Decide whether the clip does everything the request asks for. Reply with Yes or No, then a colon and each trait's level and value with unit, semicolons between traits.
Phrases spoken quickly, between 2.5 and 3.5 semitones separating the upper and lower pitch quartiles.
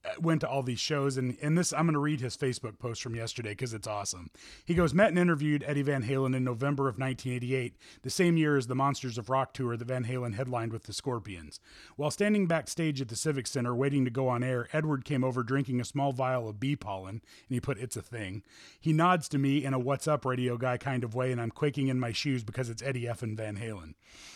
Yes: fast, 250 wpm; average, 2.9 semitones